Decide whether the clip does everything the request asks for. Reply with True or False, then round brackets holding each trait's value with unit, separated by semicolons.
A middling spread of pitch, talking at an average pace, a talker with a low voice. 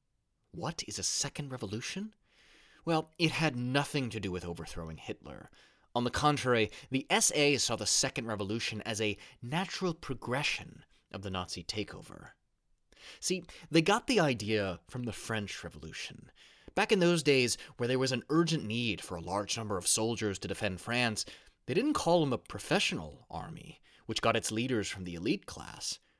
False (5.8 semitones; 170 wpm; 120 Hz)